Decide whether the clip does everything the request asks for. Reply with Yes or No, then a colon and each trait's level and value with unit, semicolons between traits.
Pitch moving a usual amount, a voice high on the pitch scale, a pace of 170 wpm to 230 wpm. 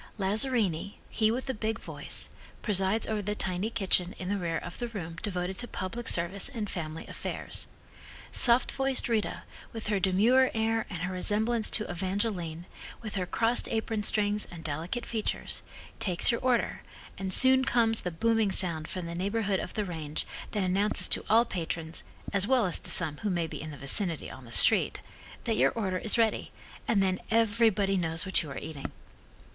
Yes: average, 4.1 semitones; high, 200 Hz; average, 185 wpm